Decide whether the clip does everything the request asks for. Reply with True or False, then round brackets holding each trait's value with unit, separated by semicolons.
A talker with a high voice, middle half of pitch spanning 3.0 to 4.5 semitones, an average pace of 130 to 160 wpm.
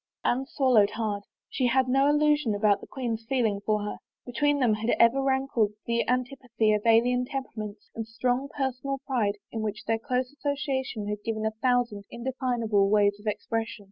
False (235 Hz; 3.5 semitones; 170 wpm)